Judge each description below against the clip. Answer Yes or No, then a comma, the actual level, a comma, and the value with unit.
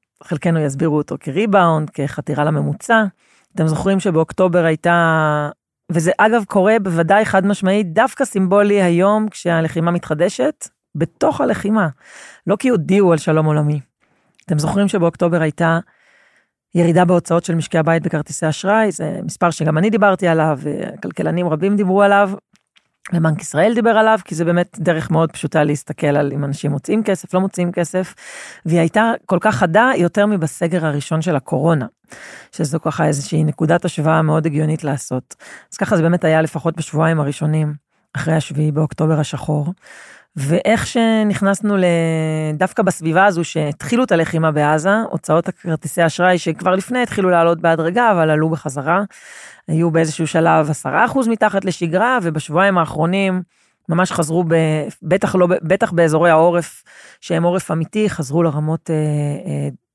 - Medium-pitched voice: Yes, medium, 170 Hz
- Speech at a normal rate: Yes, average, 140 wpm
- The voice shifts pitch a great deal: No, average, 3.6 semitones